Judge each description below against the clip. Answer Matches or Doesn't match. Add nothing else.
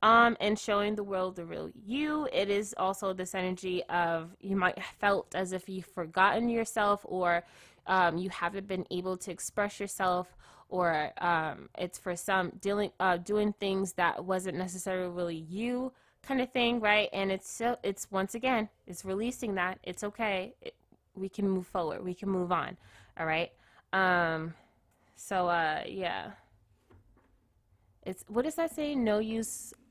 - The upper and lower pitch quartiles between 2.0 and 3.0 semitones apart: Matches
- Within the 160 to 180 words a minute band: Matches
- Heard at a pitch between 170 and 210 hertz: Matches